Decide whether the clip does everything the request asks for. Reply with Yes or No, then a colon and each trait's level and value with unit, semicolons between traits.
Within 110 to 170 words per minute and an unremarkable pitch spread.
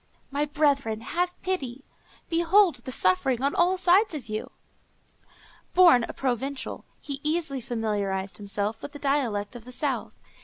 No: average, 145 wpm; wide, 6.2 semitones